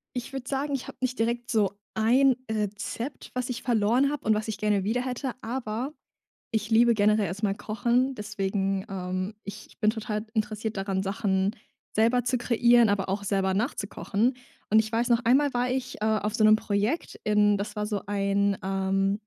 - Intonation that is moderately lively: Yes, average, 3.0 semitones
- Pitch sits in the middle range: No, high, 215 Hz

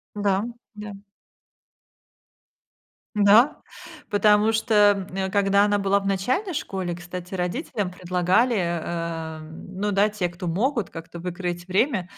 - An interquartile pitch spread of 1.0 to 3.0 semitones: Yes, narrow, 2.6 semitones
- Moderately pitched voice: No, high, 195 Hz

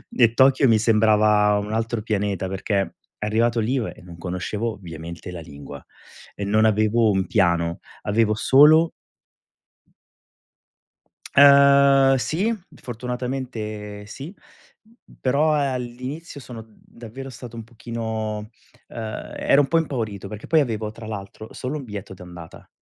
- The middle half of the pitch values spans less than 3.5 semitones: No, average, 3.9 semitones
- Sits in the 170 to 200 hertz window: No, low, 110 Hz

